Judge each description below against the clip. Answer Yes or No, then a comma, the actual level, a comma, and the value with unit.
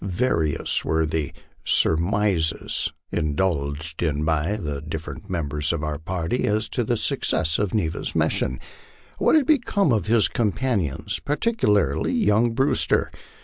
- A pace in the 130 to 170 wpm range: Yes, average, 145 wpm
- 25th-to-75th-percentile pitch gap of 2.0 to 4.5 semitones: No, wide, 5.6 semitones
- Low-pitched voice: Yes, very low, 85 Hz